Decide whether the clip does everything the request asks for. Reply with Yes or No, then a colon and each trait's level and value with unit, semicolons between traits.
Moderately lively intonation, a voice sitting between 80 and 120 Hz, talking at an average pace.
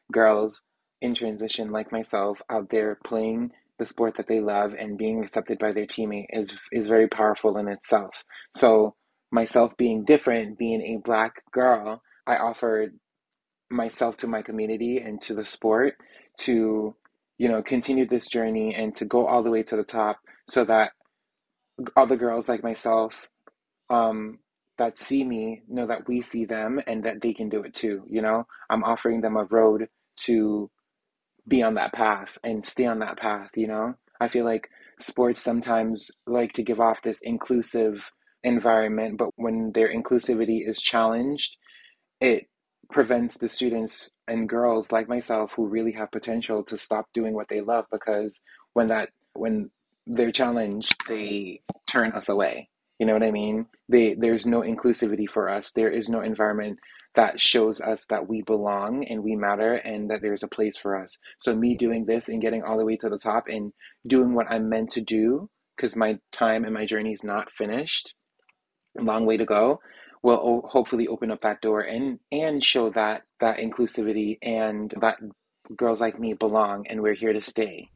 No: narrow, 1.4 semitones; low, 110 Hz; average, 180 wpm